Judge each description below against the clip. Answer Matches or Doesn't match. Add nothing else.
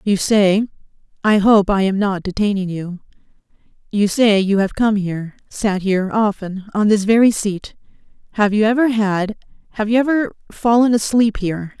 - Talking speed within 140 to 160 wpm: Matches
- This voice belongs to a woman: Matches